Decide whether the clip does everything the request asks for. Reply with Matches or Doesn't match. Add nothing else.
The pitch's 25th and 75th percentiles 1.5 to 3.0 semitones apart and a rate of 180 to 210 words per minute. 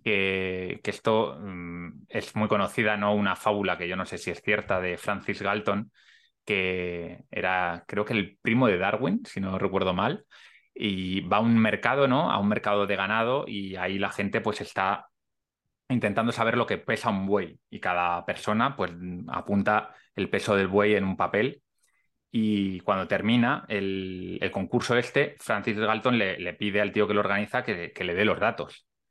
Matches